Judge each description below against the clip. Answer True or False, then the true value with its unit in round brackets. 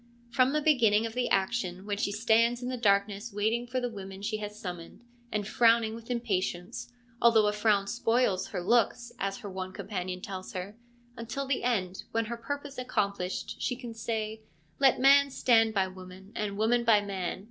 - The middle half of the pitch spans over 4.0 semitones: False (3.3 semitones)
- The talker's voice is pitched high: True (220 Hz)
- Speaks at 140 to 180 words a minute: False (200 wpm)